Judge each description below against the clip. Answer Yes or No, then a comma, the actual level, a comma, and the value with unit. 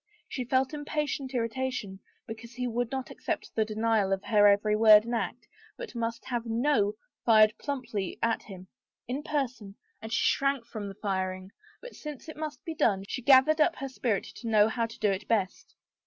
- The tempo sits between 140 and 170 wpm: No, average, 200 wpm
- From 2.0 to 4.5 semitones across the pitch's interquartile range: Yes, average, 3.9 semitones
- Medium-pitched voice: No, high, 230 Hz